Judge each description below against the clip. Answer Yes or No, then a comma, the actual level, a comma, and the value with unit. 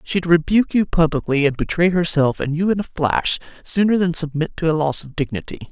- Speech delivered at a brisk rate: Yes, fast, 210 wpm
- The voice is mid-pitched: Yes, medium, 165 Hz